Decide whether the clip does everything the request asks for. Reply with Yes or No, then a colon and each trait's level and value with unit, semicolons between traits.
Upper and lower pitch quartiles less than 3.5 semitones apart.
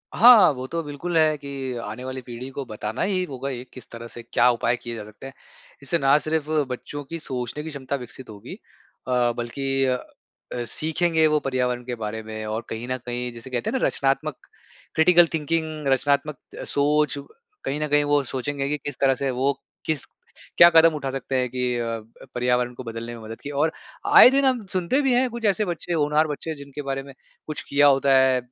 No: average, 3.8 semitones